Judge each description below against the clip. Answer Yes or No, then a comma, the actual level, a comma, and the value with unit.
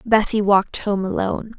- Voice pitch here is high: Yes, high, 205 Hz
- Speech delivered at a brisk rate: No, average, 150 wpm